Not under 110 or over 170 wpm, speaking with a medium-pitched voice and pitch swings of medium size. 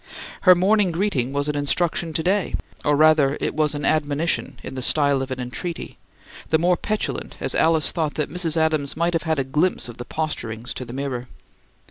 No: average, 200 wpm; medium, 155 Hz; average, 3.3 semitones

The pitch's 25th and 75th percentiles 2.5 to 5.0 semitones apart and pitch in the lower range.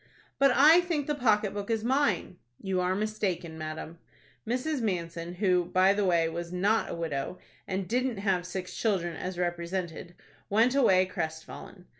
No: average, 4.3 semitones; medium, 185 Hz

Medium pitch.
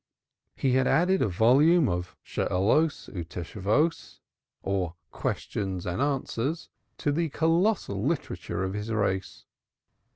No: low, 115 Hz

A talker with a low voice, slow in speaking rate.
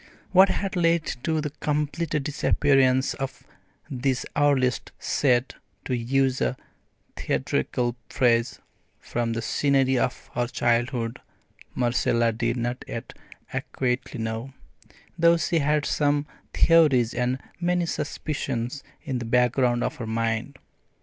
Yes: low, 130 Hz; slow, 120 wpm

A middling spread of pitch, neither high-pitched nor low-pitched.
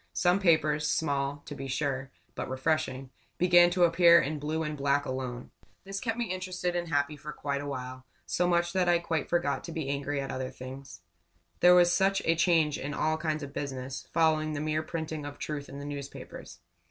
Yes: average, 3.6 semitones; medium, 150 Hz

